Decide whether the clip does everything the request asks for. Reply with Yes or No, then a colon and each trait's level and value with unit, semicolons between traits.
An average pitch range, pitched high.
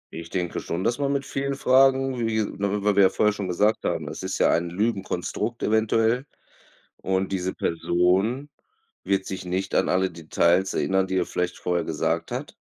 No: average, 4.2 semitones; very low, 95 Hz